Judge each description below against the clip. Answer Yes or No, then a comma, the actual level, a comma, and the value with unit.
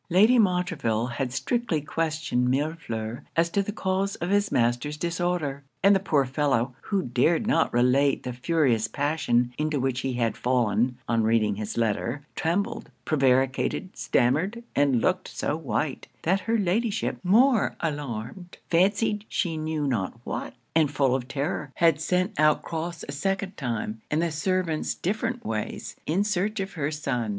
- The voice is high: No, medium, 150 Hz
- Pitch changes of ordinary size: No, wide, 6.5 semitones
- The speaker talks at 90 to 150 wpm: No, average, 160 wpm